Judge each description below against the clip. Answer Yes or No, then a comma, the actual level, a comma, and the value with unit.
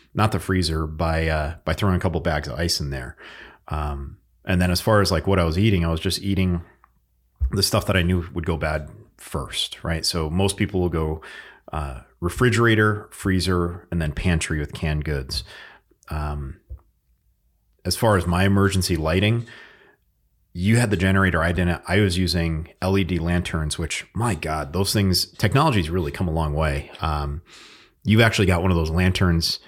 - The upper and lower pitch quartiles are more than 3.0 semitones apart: Yes, average, 3.5 semitones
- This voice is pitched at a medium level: No, very low, 85 Hz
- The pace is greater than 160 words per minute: Yes, average, 180 wpm